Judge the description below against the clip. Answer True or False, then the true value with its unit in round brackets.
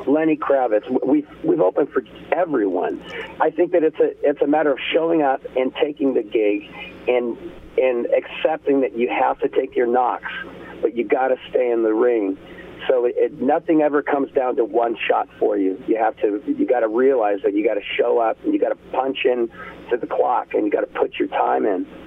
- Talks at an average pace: False (225 wpm)